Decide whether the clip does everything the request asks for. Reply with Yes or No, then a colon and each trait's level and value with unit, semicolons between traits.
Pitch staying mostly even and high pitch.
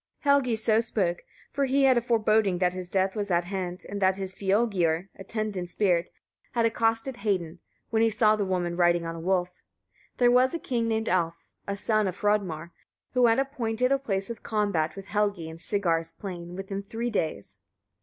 No: average, 4.1 semitones; high, 200 Hz